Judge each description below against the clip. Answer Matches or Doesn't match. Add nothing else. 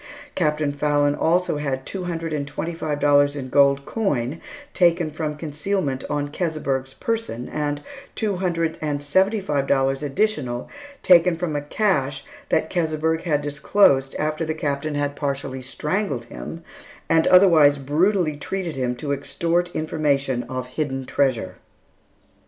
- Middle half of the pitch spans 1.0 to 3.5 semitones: Matches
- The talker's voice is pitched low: Doesn't match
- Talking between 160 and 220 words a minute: Doesn't match